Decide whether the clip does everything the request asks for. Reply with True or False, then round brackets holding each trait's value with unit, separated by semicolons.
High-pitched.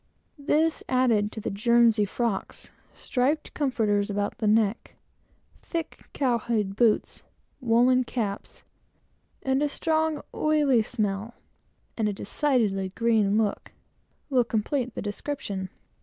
True (230 Hz)